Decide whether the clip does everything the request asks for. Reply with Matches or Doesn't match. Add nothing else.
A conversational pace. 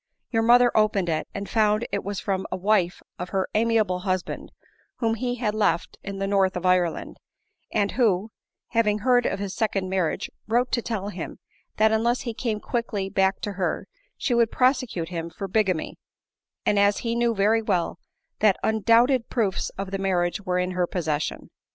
Matches